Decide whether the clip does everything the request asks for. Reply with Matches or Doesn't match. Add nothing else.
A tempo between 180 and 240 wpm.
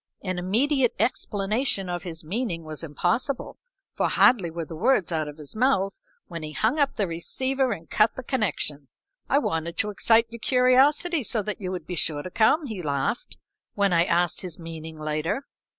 Matches